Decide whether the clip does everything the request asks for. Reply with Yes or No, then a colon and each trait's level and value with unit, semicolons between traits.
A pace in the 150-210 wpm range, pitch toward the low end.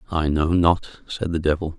Yes: average, 200 wpm; very low, 85 Hz